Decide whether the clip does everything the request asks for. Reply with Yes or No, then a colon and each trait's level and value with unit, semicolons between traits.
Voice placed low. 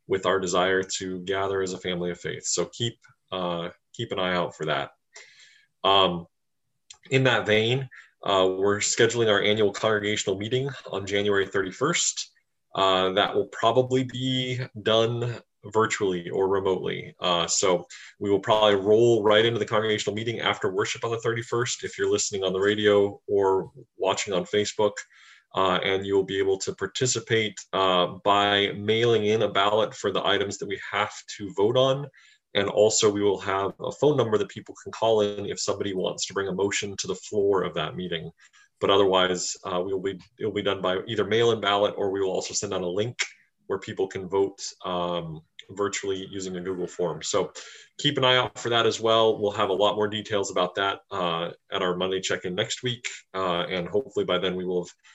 Yes: low, 100 Hz